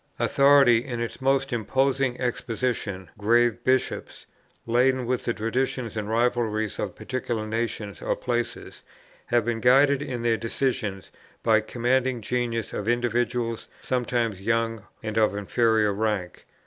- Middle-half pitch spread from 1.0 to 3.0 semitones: Yes, narrow, 2.4 semitones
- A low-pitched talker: Yes, low, 120 Hz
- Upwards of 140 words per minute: No, slow, 135 wpm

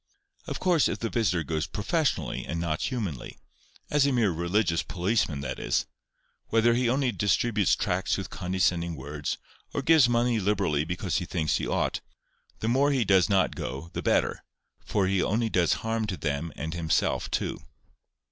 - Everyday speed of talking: Yes, average, 165 wpm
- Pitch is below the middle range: Yes, very low, 95 Hz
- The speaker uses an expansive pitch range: Yes, wide, 6.0 semitones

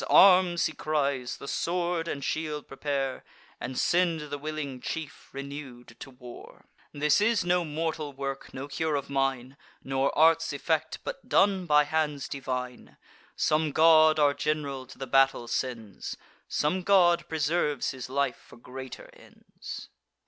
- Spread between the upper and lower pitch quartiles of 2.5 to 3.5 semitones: Yes, average, 3.1 semitones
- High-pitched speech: No, medium, 145 Hz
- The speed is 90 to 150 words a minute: Yes, average, 145 wpm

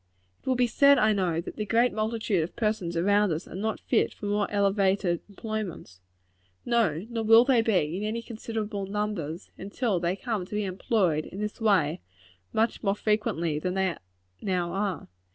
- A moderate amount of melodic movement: Yes, average, 3.2 semitones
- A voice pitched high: Yes, high, 205 Hz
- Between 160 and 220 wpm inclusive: Yes, average, 185 wpm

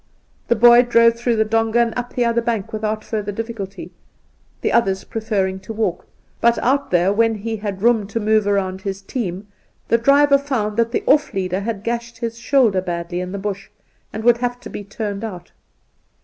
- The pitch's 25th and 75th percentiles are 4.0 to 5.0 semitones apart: No, average, 3.0 semitones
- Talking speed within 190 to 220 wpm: Yes, average, 195 wpm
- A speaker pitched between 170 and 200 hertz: No, high, 220 Hz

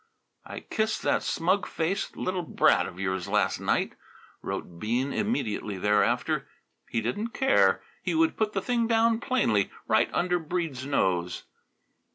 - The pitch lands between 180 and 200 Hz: No, medium, 165 Hz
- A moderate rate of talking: Yes, average, 145 wpm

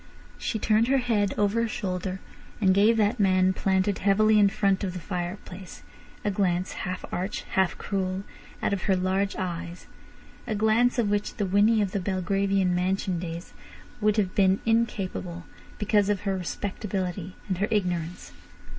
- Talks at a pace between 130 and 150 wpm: No, average, 160 wpm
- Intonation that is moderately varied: No, narrow, 2.2 semitones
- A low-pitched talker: No, high, 195 Hz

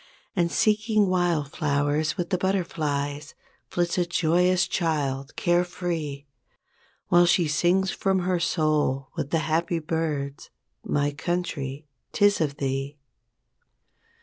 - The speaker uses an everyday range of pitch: Yes, average, 3.5 semitones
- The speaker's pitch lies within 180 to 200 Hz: No, medium, 165 Hz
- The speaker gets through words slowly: Yes, slow, 120 wpm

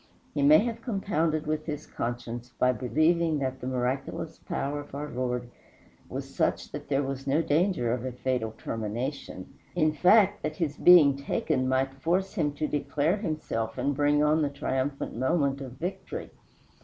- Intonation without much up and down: No, average, 3.3 semitones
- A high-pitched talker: No, medium, 145 Hz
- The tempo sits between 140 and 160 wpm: No, average, 170 wpm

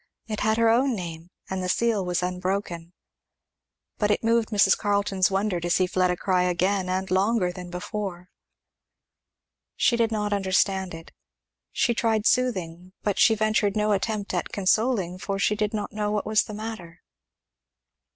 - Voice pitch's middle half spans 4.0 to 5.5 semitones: No, average, 2.9 semitones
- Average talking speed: Yes, average, 160 wpm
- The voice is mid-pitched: No, high, 200 Hz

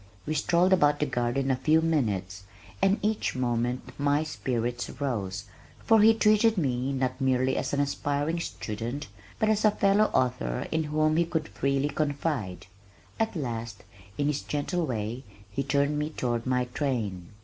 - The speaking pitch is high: No, medium, 140 Hz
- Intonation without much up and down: No, average, 4.5 semitones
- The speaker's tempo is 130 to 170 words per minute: Yes, average, 160 wpm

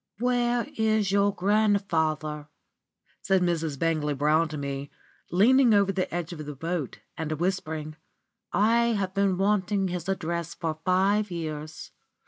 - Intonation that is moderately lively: Yes, average, 4.4 semitones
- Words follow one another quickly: No, slow, 135 wpm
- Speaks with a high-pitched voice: No, medium, 180 Hz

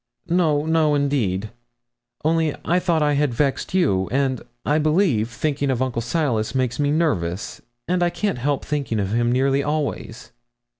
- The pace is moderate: Yes, average, 160 wpm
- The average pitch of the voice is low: No, medium, 145 Hz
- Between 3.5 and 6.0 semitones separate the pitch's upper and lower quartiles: Yes, average, 4.5 semitones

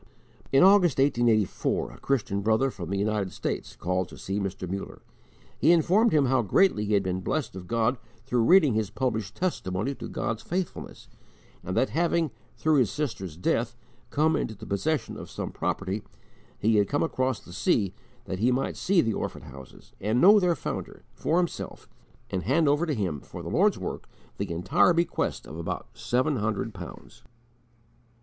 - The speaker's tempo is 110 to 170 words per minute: No, average, 180 wpm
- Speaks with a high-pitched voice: No, low, 115 Hz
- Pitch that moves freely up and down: Yes, wide, 7.7 semitones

